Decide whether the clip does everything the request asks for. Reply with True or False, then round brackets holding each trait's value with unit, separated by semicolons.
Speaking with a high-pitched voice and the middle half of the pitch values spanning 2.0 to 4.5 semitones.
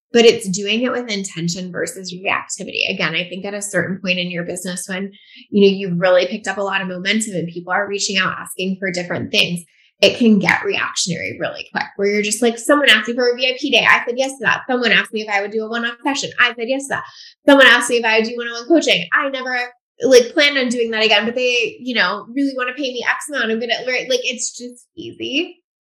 False (230 Hz; 5.0 semitones)